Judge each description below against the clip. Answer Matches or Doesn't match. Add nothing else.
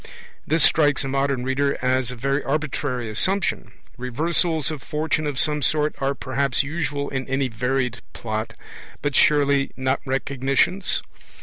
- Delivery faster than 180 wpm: Doesn't match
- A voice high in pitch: Doesn't match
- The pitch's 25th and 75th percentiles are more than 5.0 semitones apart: Doesn't match